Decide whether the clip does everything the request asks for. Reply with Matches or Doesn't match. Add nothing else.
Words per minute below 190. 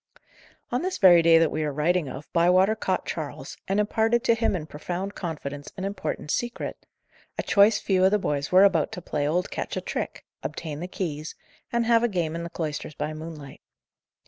Doesn't match